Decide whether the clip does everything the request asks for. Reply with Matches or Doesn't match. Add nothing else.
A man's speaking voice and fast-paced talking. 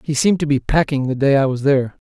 Matches